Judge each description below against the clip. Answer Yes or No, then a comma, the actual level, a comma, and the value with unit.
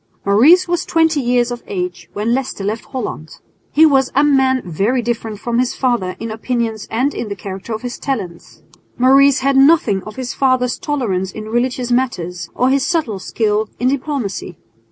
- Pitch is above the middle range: Yes, high, 240 Hz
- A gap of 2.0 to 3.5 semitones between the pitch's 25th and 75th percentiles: No, average, 4.3 semitones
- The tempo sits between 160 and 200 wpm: Yes, average, 175 wpm